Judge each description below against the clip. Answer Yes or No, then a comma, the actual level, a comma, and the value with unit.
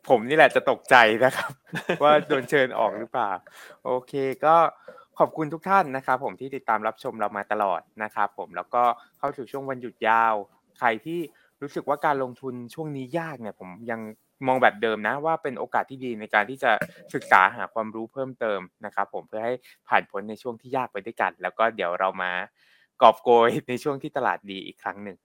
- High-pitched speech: No, low, 125 Hz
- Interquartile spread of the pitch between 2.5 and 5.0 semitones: Yes, average, 4.7 semitones